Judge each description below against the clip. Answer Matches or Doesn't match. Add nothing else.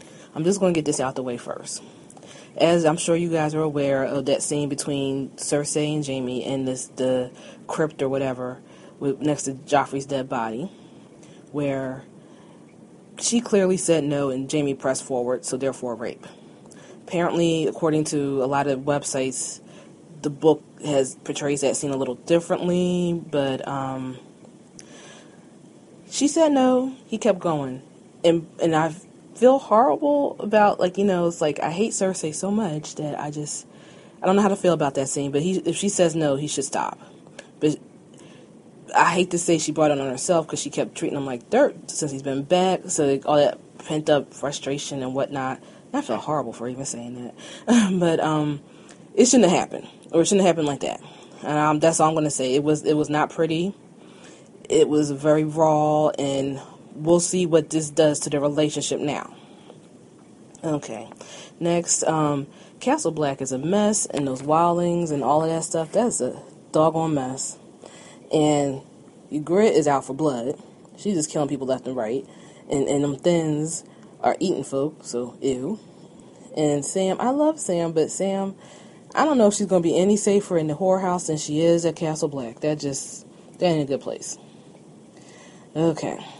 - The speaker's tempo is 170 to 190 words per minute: Matches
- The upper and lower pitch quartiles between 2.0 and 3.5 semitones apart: Doesn't match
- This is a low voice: Doesn't match